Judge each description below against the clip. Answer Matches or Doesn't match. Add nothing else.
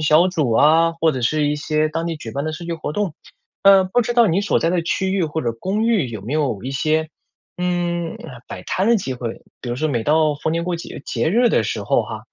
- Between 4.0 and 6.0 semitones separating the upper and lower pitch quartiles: Doesn't match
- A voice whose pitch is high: Doesn't match